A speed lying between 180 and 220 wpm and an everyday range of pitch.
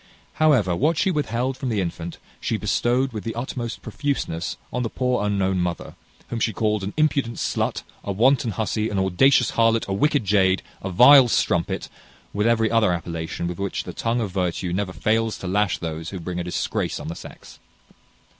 Yes: average, 190 wpm; average, 4.7 semitones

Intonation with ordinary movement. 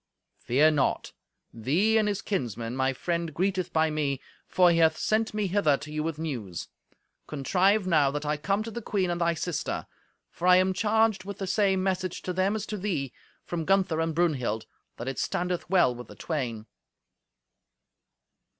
Yes: average, 4.7 semitones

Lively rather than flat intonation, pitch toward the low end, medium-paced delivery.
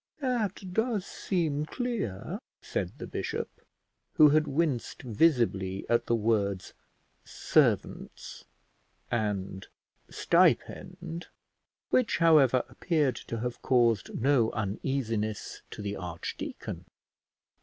No: wide, 7.6 semitones; low, 125 Hz; slow, 95 wpm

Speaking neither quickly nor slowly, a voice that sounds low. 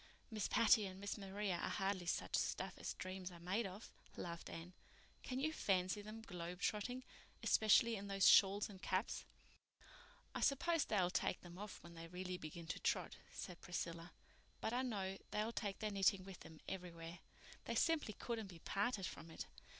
No: average, 175 wpm; high, 195 Hz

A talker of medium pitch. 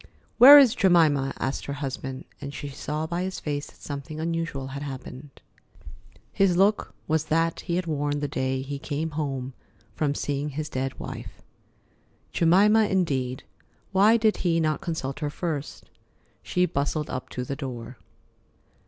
Yes: medium, 150 Hz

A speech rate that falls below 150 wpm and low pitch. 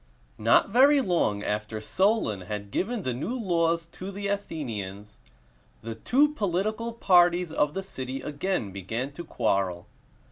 No: average, 140 wpm; medium, 165 Hz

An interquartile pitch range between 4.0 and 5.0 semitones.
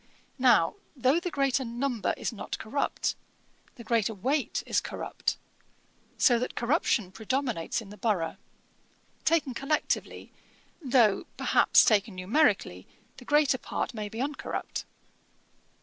Yes: average, 4.6 semitones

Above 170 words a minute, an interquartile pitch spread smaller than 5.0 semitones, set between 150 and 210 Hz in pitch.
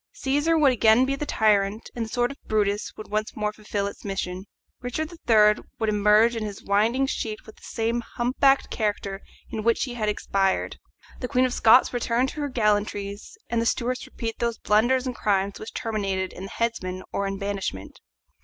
No: average, 195 wpm; average, 3.3 semitones; high, 220 Hz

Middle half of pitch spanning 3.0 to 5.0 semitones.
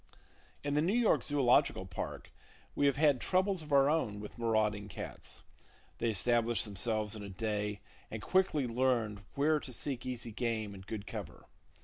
No: wide, 5.4 semitones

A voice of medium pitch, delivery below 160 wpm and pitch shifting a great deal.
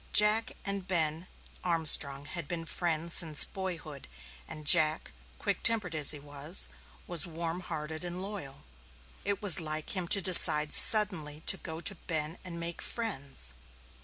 No: medium, 165 Hz; average, 150 wpm; average, 3.3 semitones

